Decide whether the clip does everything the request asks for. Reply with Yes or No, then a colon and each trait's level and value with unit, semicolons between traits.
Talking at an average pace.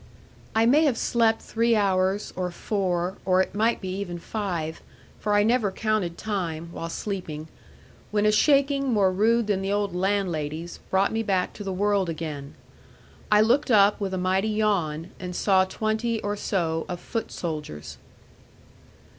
Yes: average, 165 wpm